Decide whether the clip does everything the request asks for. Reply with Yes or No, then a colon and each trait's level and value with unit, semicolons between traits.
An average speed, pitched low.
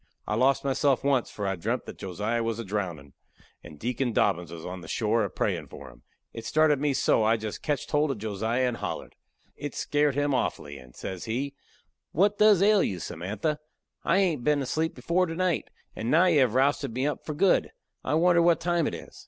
No: fast, 220 wpm; low, 130 Hz